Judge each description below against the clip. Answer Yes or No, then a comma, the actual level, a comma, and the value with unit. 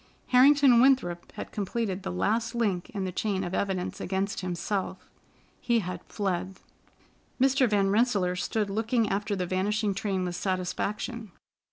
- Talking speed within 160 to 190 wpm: No, average, 145 wpm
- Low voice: No, high, 200 Hz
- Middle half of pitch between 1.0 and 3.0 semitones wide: No, average, 3.7 semitones